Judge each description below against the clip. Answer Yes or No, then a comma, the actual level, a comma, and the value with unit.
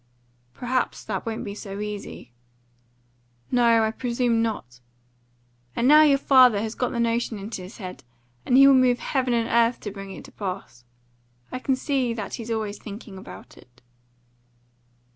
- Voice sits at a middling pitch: No, high, 230 Hz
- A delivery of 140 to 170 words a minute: Yes, average, 165 wpm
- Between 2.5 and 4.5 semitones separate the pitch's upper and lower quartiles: Yes, average, 3.6 semitones